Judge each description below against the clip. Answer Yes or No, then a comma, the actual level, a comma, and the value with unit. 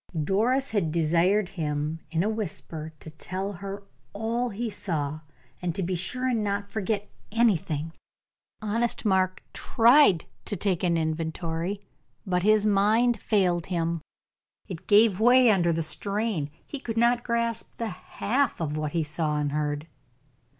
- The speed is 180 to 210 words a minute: No, average, 145 wpm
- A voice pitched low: No, high, 195 Hz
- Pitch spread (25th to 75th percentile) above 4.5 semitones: Yes, average, 5.1 semitones